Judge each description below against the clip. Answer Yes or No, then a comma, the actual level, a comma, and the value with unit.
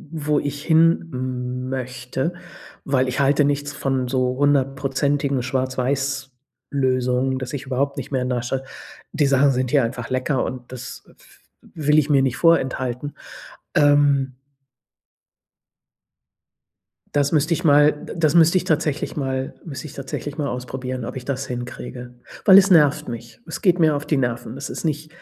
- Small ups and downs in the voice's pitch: Yes, narrow, 2.3 semitones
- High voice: No, low, 135 Hz